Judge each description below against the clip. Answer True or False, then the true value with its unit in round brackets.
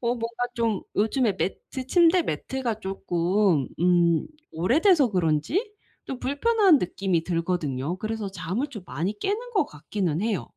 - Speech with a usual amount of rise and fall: False (7.2 semitones)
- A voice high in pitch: True (210 Hz)